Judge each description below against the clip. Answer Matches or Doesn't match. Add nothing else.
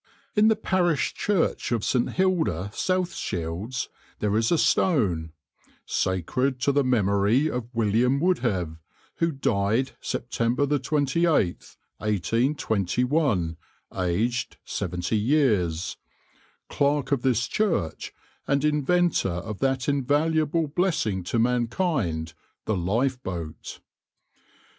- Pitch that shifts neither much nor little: Doesn't match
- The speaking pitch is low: Matches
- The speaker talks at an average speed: Doesn't match